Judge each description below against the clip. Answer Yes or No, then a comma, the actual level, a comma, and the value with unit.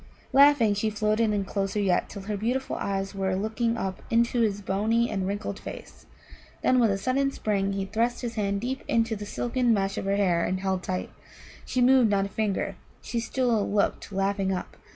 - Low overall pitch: No, high, 210 Hz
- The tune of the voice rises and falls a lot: No, average, 3.1 semitones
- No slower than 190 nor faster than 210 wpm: Yes, average, 195 wpm